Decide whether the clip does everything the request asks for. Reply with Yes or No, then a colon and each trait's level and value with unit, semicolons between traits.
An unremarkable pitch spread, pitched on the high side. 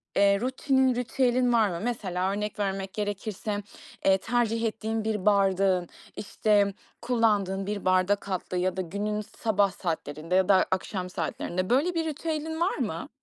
Yes: average, 3.4 semitones; high, 205 Hz